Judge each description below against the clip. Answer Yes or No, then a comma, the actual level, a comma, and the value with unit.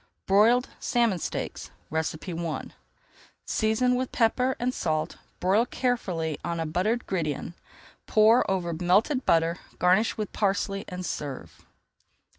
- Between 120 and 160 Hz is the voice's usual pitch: No, high, 190 Hz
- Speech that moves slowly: Yes, slow, 115 wpm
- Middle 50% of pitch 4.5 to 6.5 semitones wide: Yes, wide, 5.6 semitones